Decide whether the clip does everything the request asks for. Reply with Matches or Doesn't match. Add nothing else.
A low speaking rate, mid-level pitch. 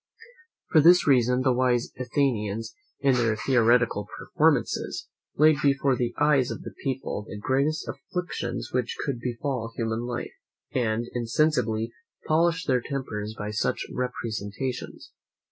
Doesn't match